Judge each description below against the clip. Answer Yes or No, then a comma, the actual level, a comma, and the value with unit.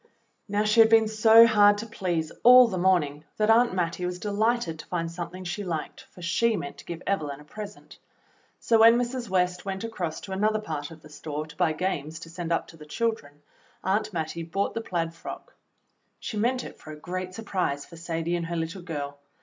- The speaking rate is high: Yes, fast, 215 wpm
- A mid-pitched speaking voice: Yes, medium, 180 Hz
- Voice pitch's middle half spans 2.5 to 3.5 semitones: No, average, 4.7 semitones